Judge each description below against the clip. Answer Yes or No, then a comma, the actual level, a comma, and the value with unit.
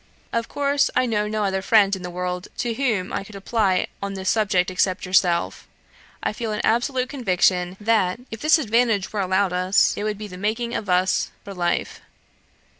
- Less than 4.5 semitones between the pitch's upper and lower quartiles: Yes, average, 3.6 semitones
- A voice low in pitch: No, high, 200 Hz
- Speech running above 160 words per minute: Yes, average, 190 wpm